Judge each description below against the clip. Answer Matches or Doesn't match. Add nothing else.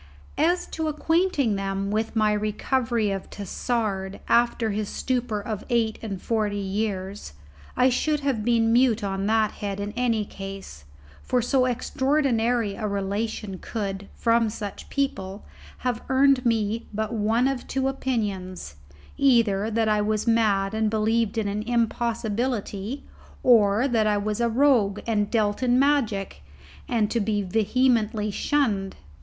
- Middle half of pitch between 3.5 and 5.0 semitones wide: Doesn't match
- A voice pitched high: Matches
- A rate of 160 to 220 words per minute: Doesn't match